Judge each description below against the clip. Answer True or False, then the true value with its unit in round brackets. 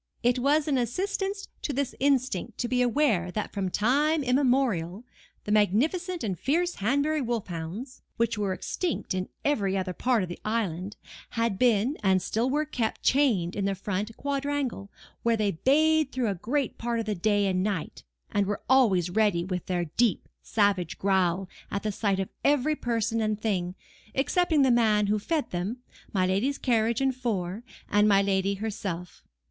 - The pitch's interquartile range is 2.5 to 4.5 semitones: False (5.4 semitones)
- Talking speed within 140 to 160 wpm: False (175 wpm)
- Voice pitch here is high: True (220 Hz)